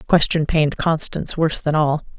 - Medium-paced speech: Yes, average, 190 wpm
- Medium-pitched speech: Yes, medium, 155 Hz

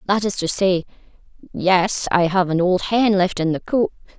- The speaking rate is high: No, average, 170 wpm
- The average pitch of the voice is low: No, medium, 185 Hz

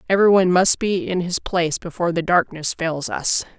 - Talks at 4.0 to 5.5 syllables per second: No, 5.8 syllables/s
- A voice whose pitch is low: No, medium, 175 Hz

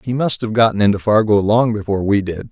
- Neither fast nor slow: No, fast, 240 wpm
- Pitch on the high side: No, low, 105 Hz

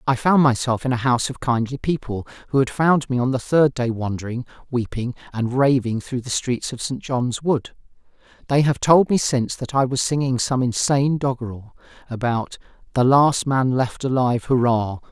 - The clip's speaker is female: No, male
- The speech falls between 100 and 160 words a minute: No, average, 185 wpm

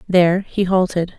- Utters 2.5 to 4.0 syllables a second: No, 4.9 syllables/s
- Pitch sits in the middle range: Yes, medium, 180 Hz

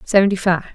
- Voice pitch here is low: No, medium, 185 Hz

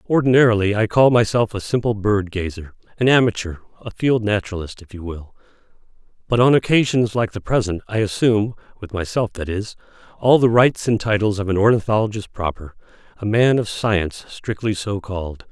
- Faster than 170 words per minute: No, average, 160 wpm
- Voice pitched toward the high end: No, low, 105 Hz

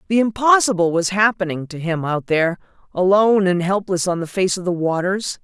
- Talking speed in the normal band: Yes, average, 190 wpm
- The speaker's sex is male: No, female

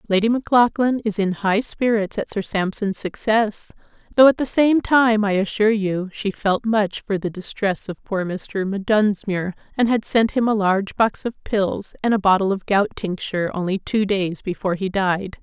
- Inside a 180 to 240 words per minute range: Yes, average, 190 wpm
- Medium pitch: No, high, 205 Hz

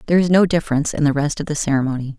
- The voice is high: No, medium, 150 Hz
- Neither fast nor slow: No, fast, 275 wpm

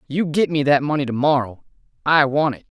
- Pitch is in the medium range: Yes, medium, 145 Hz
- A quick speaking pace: Yes, fast, 215 wpm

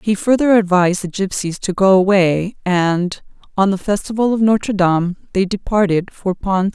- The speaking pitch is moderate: No, high, 195 Hz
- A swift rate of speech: No, average, 170 wpm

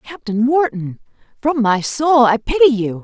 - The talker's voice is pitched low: No, very high, 250 Hz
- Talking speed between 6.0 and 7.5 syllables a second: No, 4.3 syllables/s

